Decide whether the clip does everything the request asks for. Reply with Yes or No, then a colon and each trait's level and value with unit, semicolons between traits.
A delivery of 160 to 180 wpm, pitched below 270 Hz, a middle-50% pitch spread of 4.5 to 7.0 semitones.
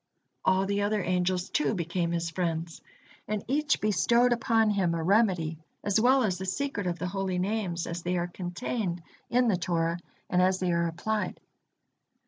No: average, 175 wpm; medium, 185 Hz; average, 3.7 semitones